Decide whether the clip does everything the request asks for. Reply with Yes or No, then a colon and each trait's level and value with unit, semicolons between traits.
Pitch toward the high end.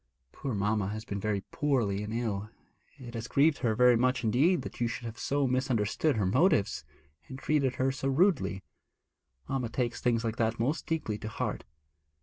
No: low, 120 Hz